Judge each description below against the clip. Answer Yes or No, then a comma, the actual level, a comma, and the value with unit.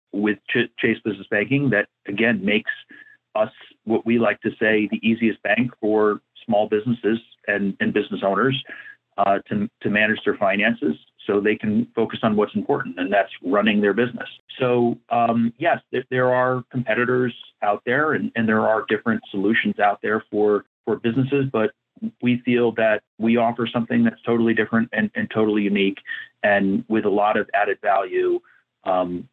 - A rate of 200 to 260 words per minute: No, average, 170 wpm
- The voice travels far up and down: No, average, 2.8 semitones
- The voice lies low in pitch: Yes, low, 115 Hz